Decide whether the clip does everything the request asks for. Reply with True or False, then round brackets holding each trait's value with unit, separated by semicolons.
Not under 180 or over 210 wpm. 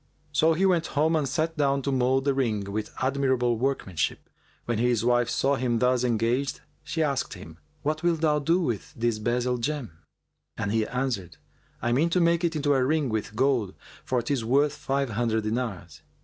True (190 wpm)